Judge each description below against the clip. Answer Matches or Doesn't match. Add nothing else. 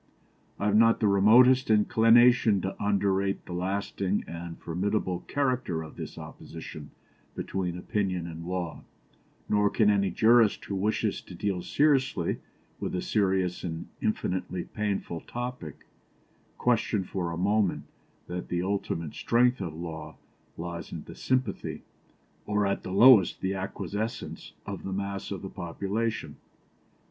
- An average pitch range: Matches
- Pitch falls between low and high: Doesn't match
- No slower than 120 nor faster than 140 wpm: Matches